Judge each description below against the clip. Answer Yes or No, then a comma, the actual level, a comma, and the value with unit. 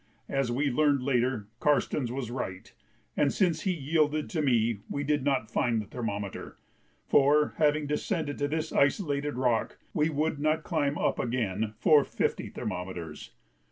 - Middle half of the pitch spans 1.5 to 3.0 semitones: No, average, 4.2 semitones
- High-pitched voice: No, medium, 140 Hz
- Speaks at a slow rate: No, average, 155 wpm